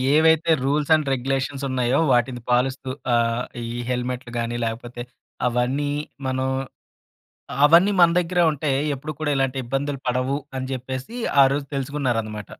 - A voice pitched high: No, low, 130 Hz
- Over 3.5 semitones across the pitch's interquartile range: No, average, 2.9 semitones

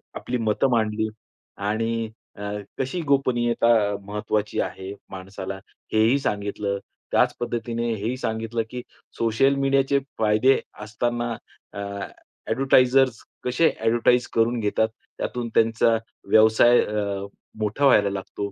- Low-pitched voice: Yes, low, 115 Hz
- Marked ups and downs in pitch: No, average, 2.7 semitones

